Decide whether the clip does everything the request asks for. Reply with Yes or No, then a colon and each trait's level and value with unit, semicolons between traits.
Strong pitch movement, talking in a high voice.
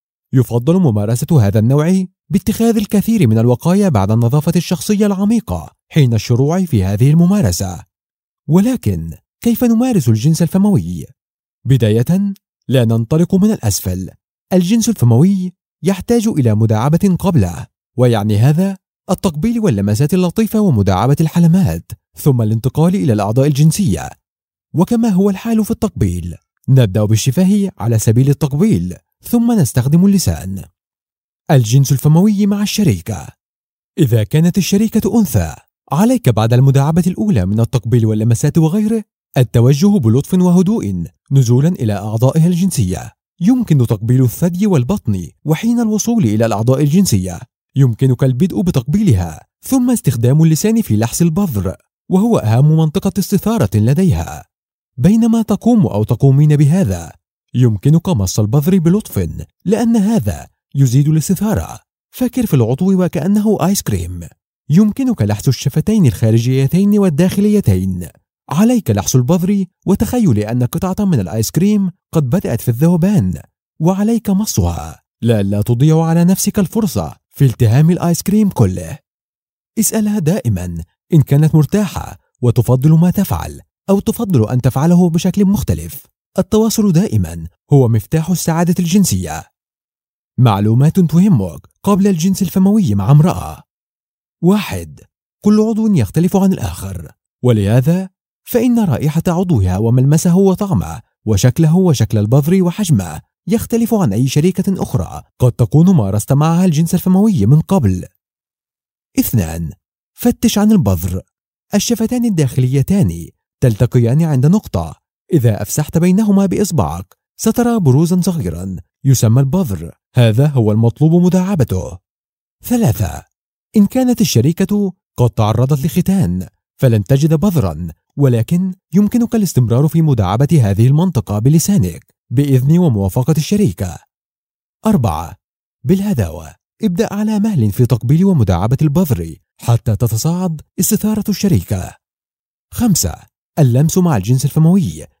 No: wide, 9.0 semitones; medium, 155 Hz